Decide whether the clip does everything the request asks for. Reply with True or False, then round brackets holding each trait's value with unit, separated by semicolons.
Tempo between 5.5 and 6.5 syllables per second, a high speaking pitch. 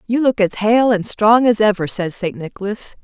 False (4.9 syllables/s; 210 Hz)